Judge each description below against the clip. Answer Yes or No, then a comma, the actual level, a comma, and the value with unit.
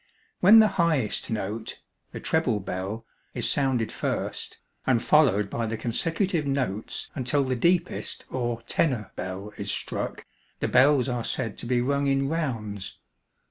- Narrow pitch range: No, average, 5.0 semitones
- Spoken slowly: No, average, 145 wpm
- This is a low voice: Yes, low, 125 Hz